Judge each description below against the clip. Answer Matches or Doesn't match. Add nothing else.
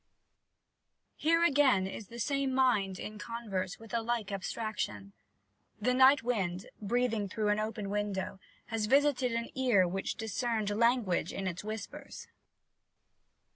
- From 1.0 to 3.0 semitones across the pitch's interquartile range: Doesn't match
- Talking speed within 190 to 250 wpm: Doesn't match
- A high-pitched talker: Matches